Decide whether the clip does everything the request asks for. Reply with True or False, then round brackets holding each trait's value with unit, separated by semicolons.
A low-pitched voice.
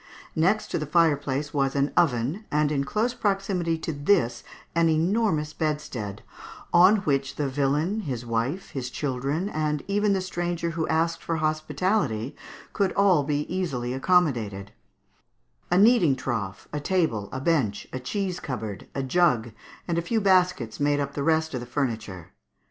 False (150 Hz)